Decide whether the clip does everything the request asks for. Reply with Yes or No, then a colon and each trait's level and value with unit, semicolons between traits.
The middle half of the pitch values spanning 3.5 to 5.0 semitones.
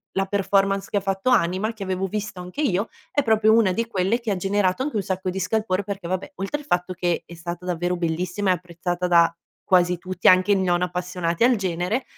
No: narrow, 2.4 semitones